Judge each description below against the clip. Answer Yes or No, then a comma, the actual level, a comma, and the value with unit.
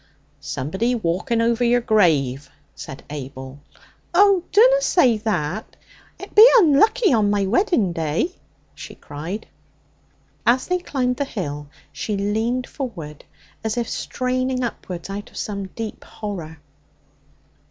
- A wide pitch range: Yes, wide, 7.3 semitones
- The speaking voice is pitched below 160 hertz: No, high, 220 Hz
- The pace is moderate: No, slow, 125 wpm